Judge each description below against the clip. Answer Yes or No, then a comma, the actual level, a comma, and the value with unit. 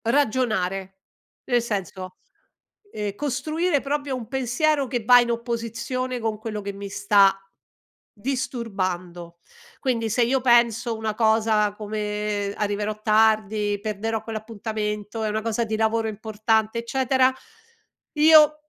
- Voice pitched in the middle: No, high, 220 Hz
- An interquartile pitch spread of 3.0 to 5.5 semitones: No, narrow, 2.6 semitones